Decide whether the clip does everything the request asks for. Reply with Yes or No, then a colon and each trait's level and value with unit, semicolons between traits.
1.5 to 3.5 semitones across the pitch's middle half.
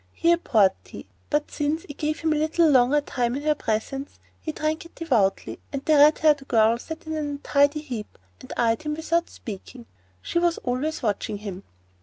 No: average, 4.4 semitones